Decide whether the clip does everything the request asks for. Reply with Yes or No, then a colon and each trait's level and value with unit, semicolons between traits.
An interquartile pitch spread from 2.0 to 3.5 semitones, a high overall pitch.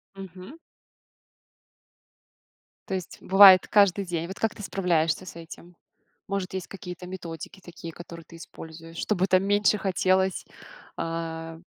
No: narrow, 2.5 semitones; medium, 180 Hz